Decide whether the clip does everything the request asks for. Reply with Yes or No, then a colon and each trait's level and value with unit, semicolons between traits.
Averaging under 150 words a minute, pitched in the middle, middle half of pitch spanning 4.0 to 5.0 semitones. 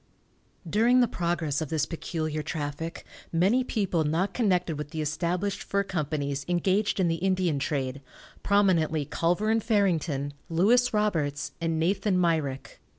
Yes: average, 140 wpm; medium, 170 Hz; average, 4.6 semitones